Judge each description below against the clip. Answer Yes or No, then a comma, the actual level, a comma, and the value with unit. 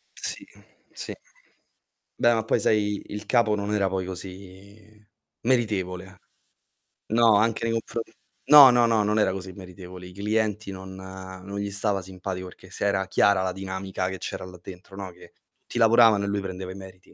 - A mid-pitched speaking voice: No, low, 100 Hz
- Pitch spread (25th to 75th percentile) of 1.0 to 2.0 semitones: No, narrow, 2.4 semitones